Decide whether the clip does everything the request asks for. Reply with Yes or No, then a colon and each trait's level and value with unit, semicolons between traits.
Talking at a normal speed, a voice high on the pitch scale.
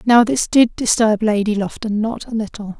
Yes: average, 195 wpm; high, 220 Hz